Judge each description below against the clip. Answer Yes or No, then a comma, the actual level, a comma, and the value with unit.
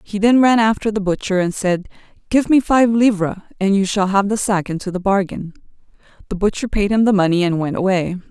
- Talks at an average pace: No, fast, 215 wpm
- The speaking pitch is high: Yes, high, 200 Hz